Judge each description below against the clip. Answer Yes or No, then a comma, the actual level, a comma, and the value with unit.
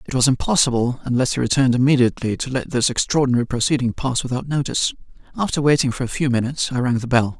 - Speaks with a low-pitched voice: Yes, low, 130 Hz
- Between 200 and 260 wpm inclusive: Yes, fast, 205 wpm